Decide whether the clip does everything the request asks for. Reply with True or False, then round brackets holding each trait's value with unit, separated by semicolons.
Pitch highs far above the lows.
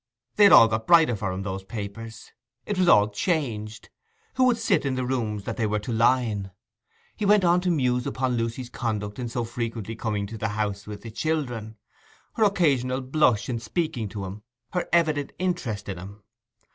True (6.6 semitones)